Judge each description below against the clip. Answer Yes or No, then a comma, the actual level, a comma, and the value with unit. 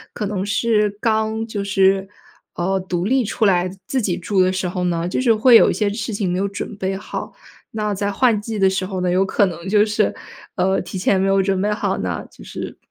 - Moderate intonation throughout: No, narrow, 2.2 semitones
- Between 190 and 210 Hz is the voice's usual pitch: Yes, high, 195 Hz